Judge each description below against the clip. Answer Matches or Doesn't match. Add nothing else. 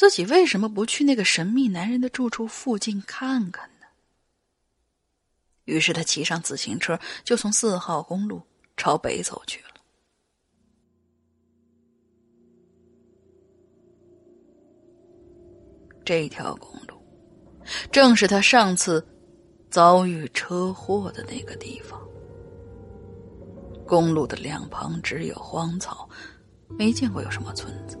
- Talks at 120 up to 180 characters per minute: Matches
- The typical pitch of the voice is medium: Matches